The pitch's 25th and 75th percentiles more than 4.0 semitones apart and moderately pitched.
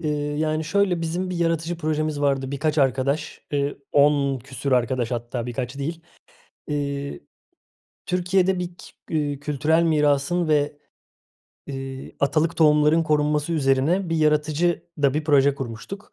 No: average, 2.8 semitones; medium, 150 Hz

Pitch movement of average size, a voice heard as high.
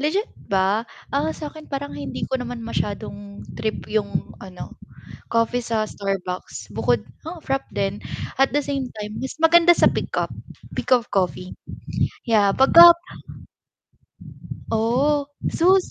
No: wide, 6.2 semitones; high, 240 Hz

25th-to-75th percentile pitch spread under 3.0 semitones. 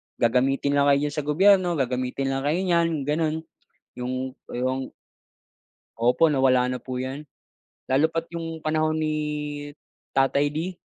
No: average, 3.4 semitones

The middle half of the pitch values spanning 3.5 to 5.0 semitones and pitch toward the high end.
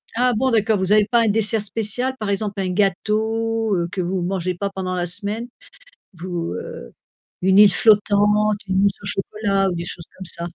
No: average, 2.7 semitones; high, 200 Hz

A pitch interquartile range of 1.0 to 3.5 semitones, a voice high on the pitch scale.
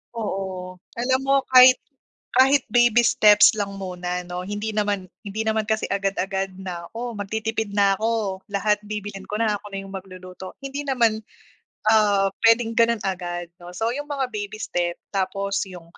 Yes: average, 3.0 semitones; high, 205 Hz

